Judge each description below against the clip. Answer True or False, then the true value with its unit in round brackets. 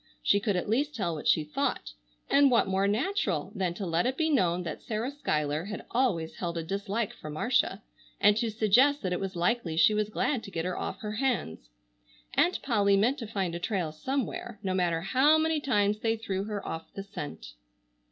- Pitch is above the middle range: True (200 Hz)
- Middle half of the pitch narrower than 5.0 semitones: False (5.6 semitones)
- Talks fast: True (210 wpm)